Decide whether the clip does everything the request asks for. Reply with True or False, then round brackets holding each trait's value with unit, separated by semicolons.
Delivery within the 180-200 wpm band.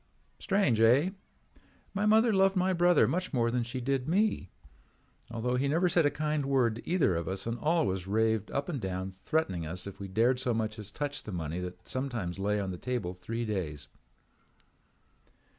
True (190 wpm)